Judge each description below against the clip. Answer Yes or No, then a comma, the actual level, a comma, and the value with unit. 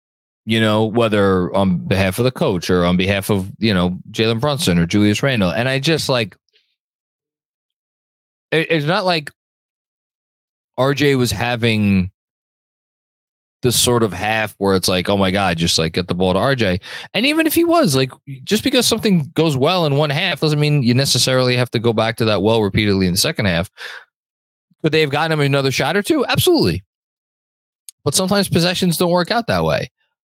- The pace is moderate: Yes, average, 185 wpm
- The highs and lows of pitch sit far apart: Yes, wide, 7.7 semitones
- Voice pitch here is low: Yes, low, 125 Hz